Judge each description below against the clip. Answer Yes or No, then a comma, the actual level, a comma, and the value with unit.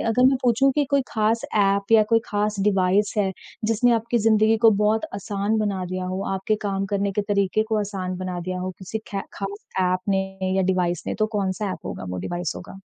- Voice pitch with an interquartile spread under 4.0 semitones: Yes, narrow, 2.4 semitones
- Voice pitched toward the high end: Yes, high, 200 Hz